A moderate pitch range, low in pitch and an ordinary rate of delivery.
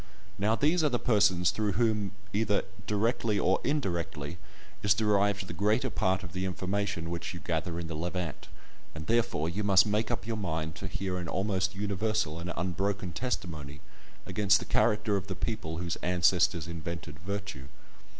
Yes: average, 3.5 semitones; very low, 95 Hz; average, 170 wpm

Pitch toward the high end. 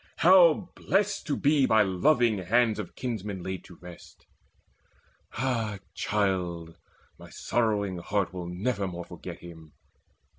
No: low, 105 Hz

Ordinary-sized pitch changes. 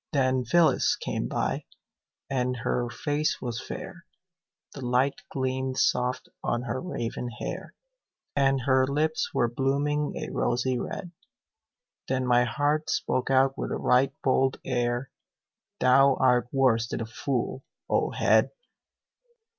No: narrow, 2.0 semitones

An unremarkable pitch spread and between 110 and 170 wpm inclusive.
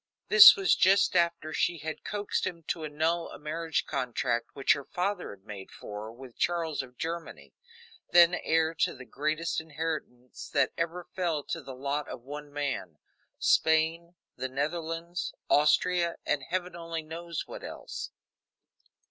Yes: average, 3.4 semitones; average, 155 wpm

